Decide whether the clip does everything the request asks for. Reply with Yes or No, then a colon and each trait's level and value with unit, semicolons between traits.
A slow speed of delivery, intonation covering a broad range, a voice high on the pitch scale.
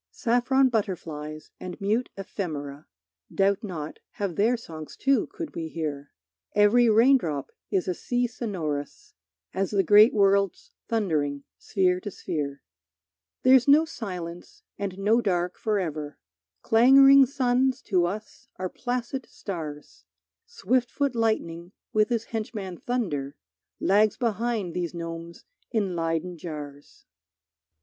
Yes: slow, 120 wpm; wide, 5.9 semitones; high, 195 Hz